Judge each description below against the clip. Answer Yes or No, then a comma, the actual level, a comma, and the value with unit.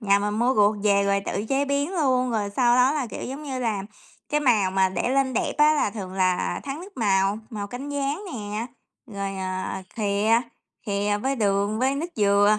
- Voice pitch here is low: No, high, 220 Hz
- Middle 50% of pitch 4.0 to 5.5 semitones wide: Yes, average, 5.1 semitones